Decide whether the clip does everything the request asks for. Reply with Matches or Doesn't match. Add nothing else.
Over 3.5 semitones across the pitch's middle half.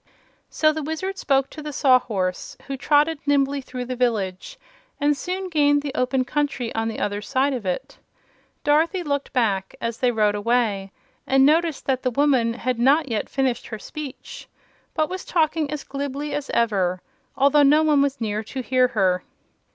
Matches